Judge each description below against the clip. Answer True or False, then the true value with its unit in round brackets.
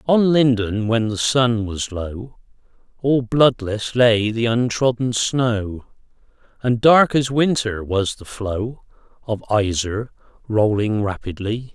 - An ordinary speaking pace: False (125 wpm)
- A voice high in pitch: False (115 Hz)